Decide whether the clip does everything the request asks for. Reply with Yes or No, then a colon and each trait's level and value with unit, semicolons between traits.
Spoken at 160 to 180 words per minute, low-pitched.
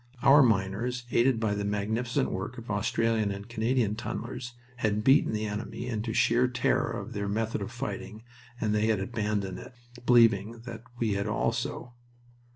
Yes: average, 165 wpm; low, 110 Hz